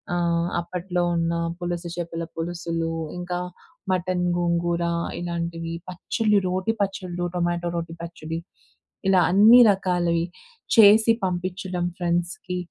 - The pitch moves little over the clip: Yes, narrow, 1.3 semitones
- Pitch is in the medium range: Yes, medium, 175 Hz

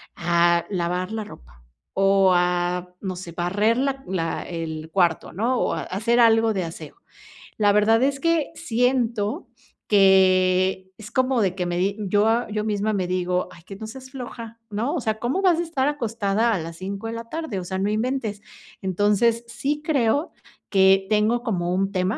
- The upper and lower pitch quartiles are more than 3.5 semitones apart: Yes, average, 4.1 semitones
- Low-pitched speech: No, high, 205 Hz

